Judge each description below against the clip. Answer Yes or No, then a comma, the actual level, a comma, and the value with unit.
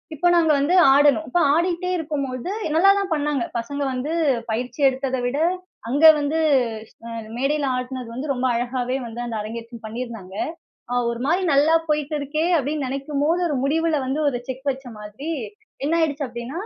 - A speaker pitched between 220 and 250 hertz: No, very high, 275 Hz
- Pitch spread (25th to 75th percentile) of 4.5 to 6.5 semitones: No, average, 3.8 semitones